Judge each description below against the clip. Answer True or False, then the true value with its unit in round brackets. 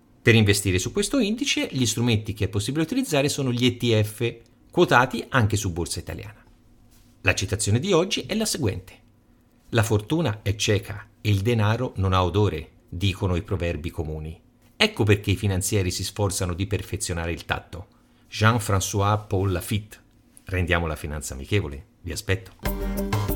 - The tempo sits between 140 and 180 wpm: True (150 wpm)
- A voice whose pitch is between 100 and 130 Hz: True (105 Hz)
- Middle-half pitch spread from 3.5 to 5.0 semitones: True (4.1 semitones)